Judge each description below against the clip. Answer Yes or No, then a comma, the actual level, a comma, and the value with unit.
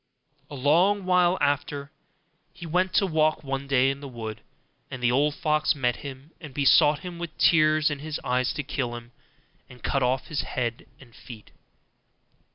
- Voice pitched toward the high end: No, medium, 145 Hz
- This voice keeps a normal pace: Yes, average, 175 wpm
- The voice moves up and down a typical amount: Yes, average, 3.3 semitones